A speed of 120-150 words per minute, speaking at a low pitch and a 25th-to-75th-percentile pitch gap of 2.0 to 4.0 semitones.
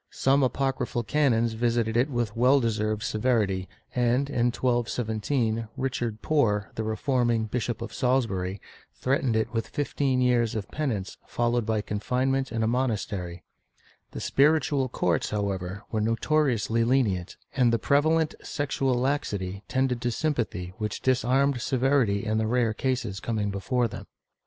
Yes: average, 140 wpm; low, 120 Hz; average, 3.4 semitones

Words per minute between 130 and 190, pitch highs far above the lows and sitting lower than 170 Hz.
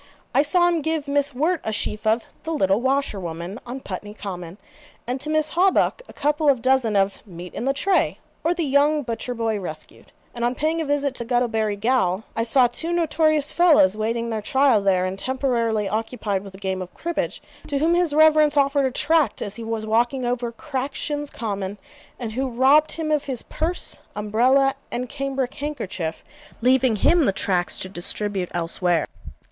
No: average, 185 wpm; wide, 5.8 semitones; very high, 250 Hz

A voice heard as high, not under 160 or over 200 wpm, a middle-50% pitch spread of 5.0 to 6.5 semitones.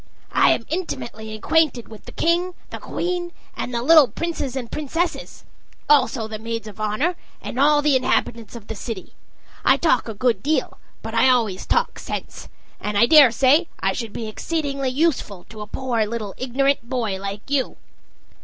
Yes: very high, 250 Hz; average, 170 wpm; wide, 5.4 semitones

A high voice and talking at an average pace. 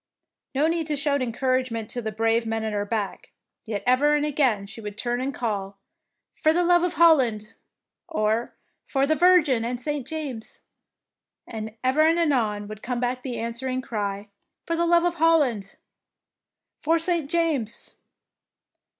Yes: very high, 255 Hz; average, 155 wpm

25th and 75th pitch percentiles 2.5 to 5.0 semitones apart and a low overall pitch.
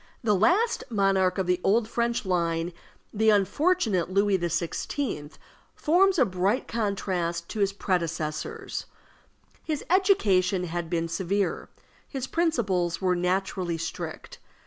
No: average, 4.7 semitones; high, 190 Hz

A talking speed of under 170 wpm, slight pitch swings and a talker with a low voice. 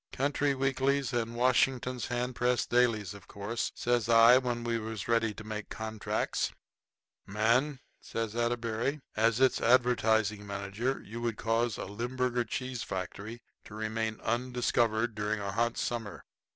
Yes: average, 140 wpm; narrow, 2.2 semitones; low, 115 Hz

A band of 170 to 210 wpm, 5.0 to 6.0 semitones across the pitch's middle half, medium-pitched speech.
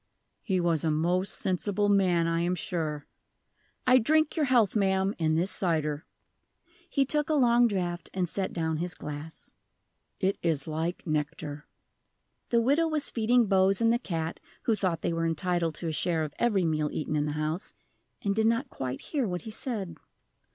Yes: average, 180 wpm; wide, 5.5 semitones; medium, 180 Hz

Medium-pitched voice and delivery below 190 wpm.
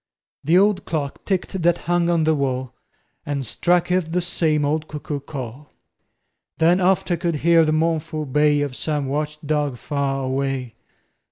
Yes: medium, 155 Hz; average, 165 wpm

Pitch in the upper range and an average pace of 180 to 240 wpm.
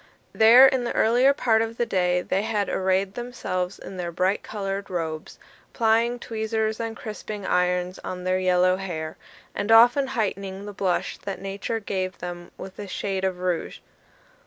No: high, 195 Hz; average, 165 wpm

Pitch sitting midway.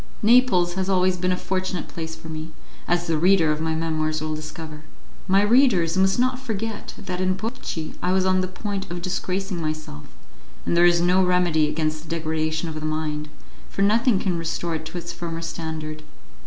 Yes: medium, 175 Hz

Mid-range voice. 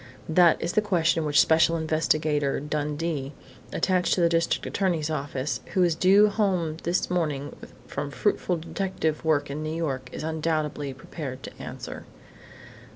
Yes: medium, 160 Hz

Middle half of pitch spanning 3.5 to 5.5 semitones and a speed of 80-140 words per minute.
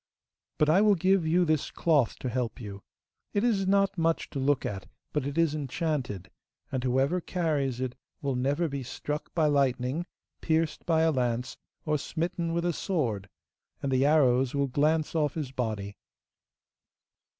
No: average, 4.3 semitones; average, 165 wpm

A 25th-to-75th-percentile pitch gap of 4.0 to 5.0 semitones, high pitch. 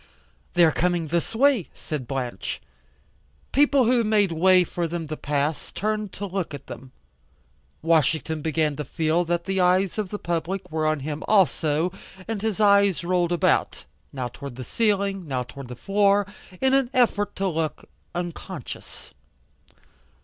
No: average, 4.5 semitones; medium, 175 Hz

